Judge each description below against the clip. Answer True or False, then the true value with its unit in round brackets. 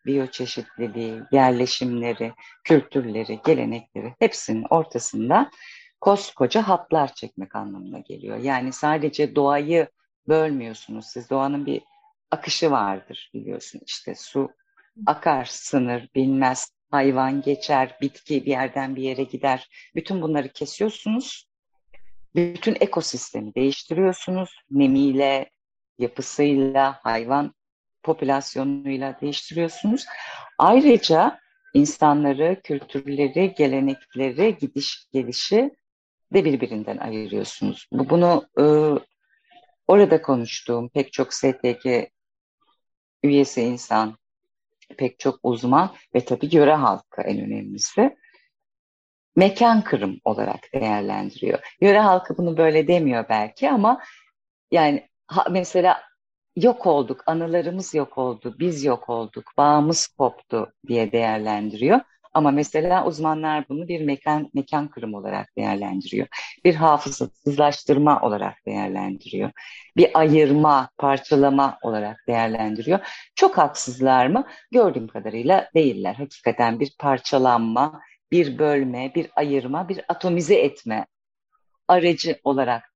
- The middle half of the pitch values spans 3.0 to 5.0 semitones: False (5.5 semitones)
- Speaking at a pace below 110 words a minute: True (100 wpm)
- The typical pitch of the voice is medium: True (145 Hz)